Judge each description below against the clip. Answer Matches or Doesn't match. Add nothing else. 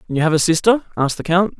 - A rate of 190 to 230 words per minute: Doesn't match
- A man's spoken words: Matches